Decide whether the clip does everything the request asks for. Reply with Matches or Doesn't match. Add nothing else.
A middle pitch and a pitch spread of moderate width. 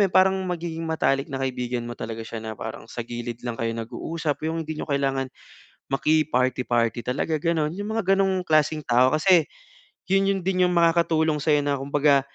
Matches